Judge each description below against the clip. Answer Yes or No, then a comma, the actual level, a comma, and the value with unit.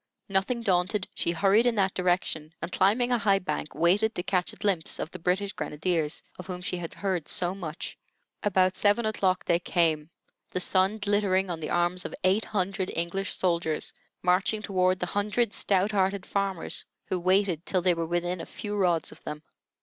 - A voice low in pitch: No, medium, 185 Hz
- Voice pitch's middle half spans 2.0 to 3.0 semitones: Yes, narrow, 2.4 semitones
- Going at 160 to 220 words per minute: Yes, average, 190 wpm